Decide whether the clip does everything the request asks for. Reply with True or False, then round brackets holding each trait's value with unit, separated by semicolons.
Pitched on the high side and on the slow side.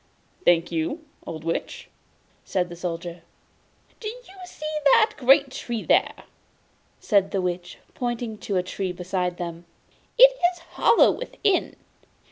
True (200 Hz; 130 wpm)